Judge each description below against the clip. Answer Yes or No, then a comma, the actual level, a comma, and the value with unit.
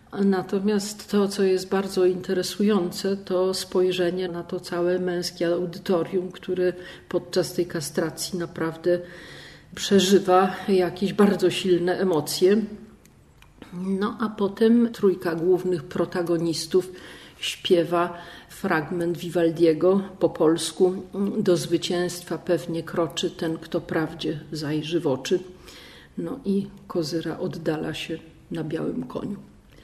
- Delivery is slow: Yes, slow, 105 wpm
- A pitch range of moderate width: No, narrow, 2.0 semitones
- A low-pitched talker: No, medium, 180 Hz